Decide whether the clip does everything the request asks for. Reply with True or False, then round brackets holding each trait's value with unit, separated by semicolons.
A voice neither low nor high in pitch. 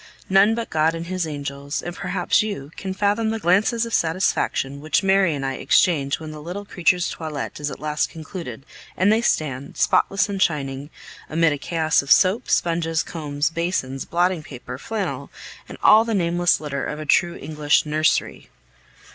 True (165 Hz)